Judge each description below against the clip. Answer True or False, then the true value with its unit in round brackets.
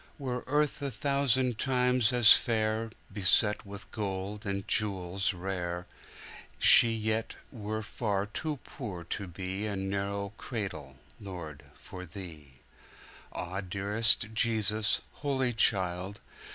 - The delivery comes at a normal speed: False (100 wpm)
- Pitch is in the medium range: False (105 Hz)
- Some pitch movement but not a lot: True (3.2 semitones)